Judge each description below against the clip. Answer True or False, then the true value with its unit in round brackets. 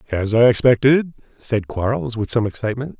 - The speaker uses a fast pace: False (160 wpm)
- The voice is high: False (115 Hz)